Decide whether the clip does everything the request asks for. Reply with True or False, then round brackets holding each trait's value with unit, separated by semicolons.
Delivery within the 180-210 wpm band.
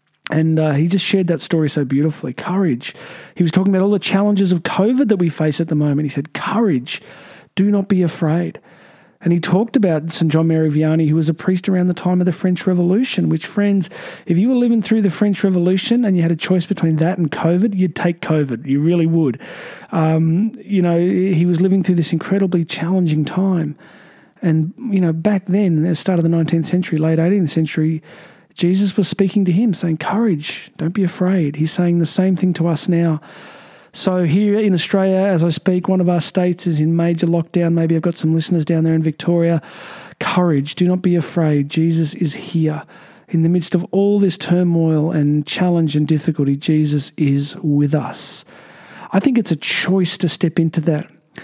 True (205 wpm)